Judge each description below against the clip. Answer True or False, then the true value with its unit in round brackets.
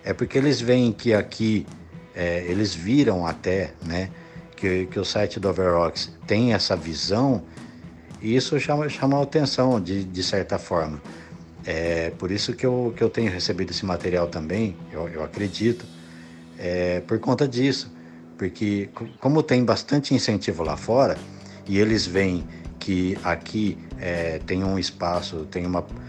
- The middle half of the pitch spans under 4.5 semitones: False (5.2 semitones)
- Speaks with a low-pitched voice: True (95 Hz)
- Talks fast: False (155 wpm)